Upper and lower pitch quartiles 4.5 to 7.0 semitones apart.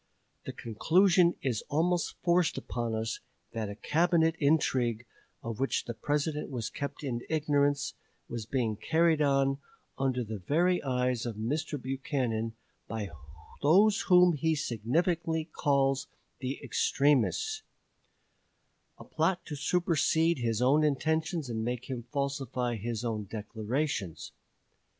Yes: average, 5.2 semitones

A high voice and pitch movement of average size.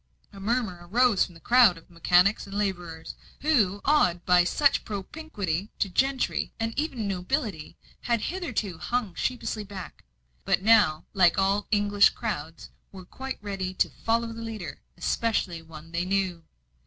Yes: high, 200 Hz; average, 4.5 semitones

